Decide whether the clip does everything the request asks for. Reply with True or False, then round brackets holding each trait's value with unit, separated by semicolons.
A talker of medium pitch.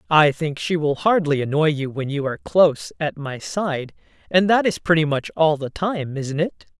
True (155 Hz)